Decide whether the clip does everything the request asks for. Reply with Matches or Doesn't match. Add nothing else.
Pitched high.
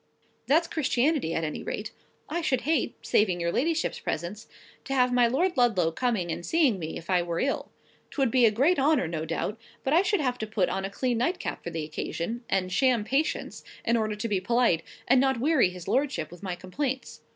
Matches